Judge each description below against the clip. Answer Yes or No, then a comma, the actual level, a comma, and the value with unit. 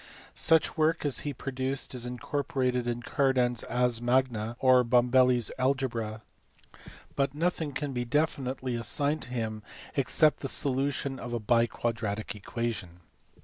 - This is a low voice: Yes, low, 125 Hz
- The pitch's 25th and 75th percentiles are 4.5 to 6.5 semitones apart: No, narrow, 2.6 semitones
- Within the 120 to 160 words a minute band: Yes, average, 145 wpm